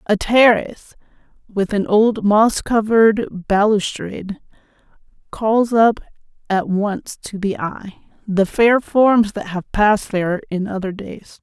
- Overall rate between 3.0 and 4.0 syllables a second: Yes, 3.9 syllables/s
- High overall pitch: Yes, high, 210 Hz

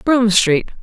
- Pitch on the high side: Yes, high, 215 Hz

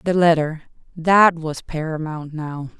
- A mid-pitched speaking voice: Yes, medium, 160 Hz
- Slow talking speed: Yes, slow, 105 wpm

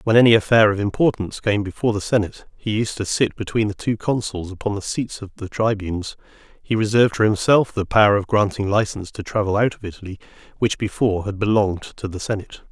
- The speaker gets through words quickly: Yes, fast, 210 wpm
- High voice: No, low, 105 Hz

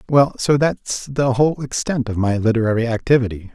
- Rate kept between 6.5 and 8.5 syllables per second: No, 5.4 syllables/s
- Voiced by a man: Yes, male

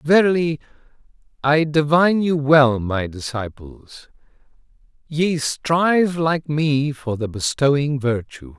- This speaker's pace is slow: Yes, slow, 105 wpm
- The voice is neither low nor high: Yes, medium, 145 Hz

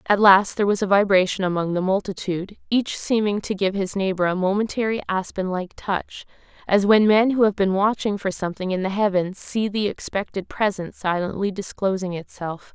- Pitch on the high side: Yes, high, 195 Hz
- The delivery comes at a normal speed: Yes, average, 185 wpm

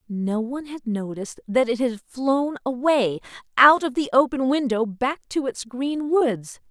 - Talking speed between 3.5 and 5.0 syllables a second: Yes, 4.3 syllables/s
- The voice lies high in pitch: Yes, very high, 255 Hz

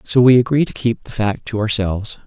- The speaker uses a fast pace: Yes, fast, 240 wpm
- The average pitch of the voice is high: No, low, 115 Hz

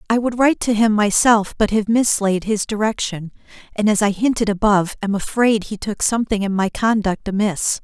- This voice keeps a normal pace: Yes, average, 190 wpm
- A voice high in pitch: Yes, high, 210 Hz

